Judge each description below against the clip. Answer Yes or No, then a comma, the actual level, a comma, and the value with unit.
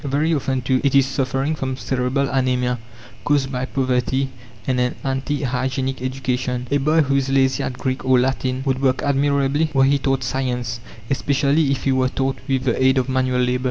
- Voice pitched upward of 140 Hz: No, low, 130 Hz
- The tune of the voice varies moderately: No, narrow, 1.3 semitones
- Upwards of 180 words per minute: Yes, average, 195 wpm